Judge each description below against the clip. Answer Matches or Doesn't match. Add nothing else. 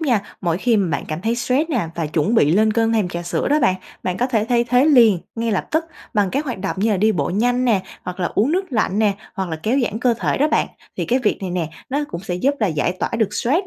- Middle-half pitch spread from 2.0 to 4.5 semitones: Doesn't match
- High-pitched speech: Matches